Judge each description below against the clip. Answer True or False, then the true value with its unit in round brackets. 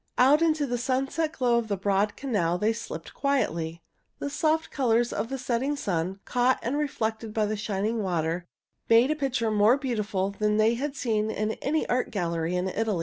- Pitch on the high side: True (225 Hz)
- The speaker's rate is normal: True (190 wpm)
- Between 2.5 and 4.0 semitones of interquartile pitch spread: False (4.7 semitones)